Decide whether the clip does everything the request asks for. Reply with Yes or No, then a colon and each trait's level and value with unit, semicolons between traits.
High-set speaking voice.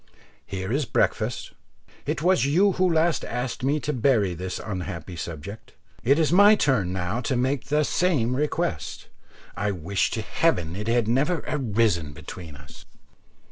No: low, 120 Hz